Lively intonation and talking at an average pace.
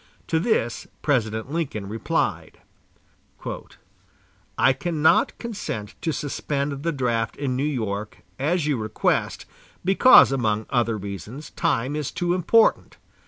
No: wide, 6.0 semitones; slow, 120 wpm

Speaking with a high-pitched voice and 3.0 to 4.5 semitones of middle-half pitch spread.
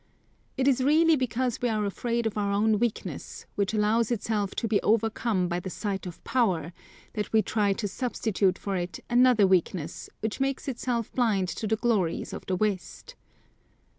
Yes: high, 215 Hz; average, 3.4 semitones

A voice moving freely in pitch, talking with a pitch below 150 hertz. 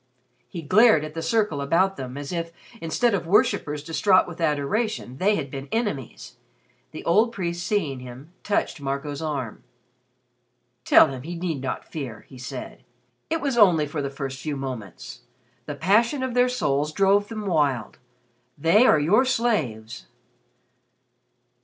No: wide, 6.7 semitones; medium, 160 Hz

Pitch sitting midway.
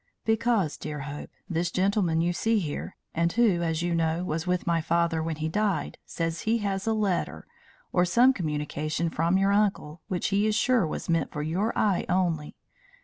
Yes: medium, 175 Hz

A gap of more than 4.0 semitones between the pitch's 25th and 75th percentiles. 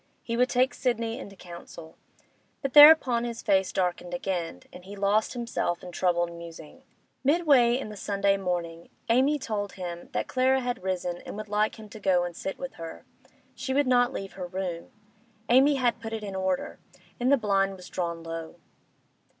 Yes: wide, 5.5 semitones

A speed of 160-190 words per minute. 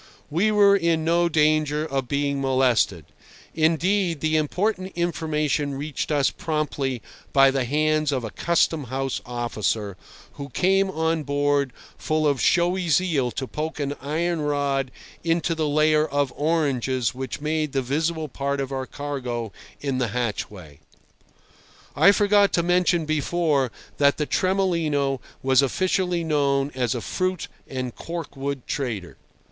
No: average, 140 wpm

